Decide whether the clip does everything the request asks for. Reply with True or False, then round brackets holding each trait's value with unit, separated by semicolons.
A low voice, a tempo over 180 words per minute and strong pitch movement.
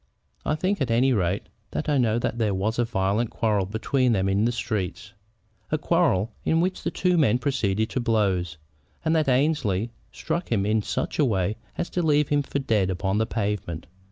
True (115 Hz; 200 wpm; 6.0 semitones)